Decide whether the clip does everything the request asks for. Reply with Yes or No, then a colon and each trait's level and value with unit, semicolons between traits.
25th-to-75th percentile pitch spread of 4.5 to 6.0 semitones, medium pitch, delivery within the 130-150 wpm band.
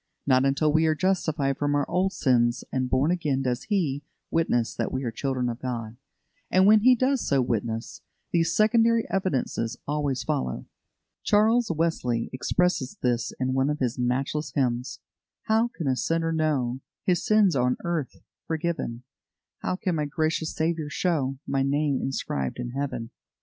No: average, 5.1 semitones; medium, 145 Hz; average, 160 wpm